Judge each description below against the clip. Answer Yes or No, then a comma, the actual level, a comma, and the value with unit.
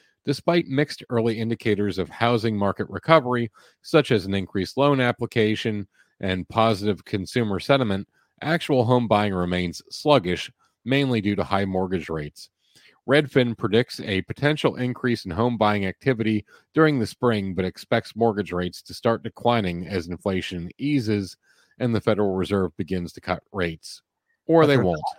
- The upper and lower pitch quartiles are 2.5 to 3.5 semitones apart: No, average, 4.8 semitones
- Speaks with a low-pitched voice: Yes, low, 110 Hz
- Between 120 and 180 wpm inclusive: Yes, average, 150 wpm